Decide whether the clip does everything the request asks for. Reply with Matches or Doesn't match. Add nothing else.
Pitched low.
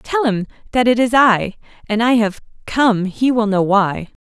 Doesn't match